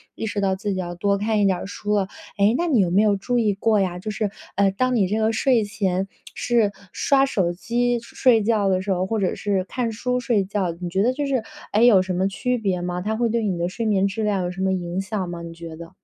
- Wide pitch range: No, average, 3.1 semitones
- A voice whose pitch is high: Yes, high, 200 Hz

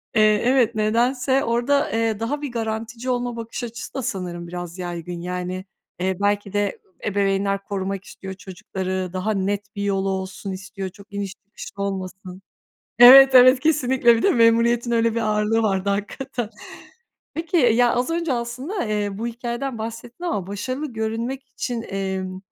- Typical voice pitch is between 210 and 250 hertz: Yes, high, 220 Hz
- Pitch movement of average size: Yes, average, 3.9 semitones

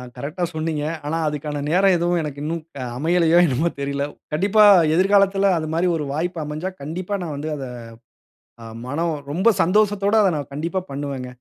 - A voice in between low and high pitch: Yes, medium, 165 Hz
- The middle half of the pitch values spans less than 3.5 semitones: No, average, 4.1 semitones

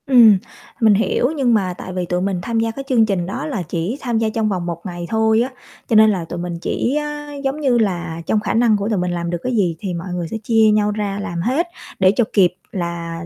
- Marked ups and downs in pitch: No, average, 4.6 semitones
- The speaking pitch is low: No, high, 205 Hz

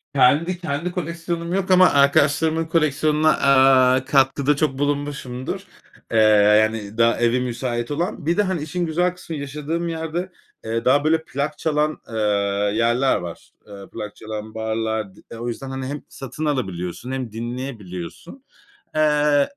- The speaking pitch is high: No, medium, 140 Hz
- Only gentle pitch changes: No, average, 5.0 semitones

